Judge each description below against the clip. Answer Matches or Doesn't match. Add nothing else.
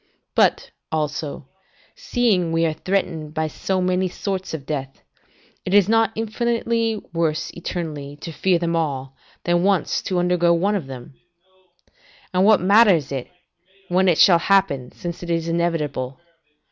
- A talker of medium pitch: Matches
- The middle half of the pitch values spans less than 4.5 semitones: Matches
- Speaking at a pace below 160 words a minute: Matches